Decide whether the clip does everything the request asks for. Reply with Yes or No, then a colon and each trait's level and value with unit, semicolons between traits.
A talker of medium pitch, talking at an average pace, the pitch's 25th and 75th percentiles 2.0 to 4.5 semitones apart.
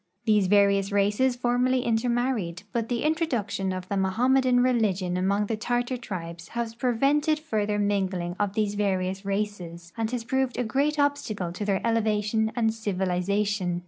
No: high, 210 Hz; average, 155 wpm; average, 4.1 semitones